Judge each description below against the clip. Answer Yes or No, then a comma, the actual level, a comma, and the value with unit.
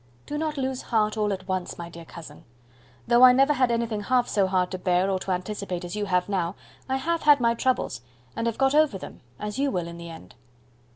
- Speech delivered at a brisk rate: Yes, fast, 235 wpm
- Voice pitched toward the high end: Yes, high, 210 Hz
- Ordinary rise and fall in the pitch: No, wide, 6.0 semitones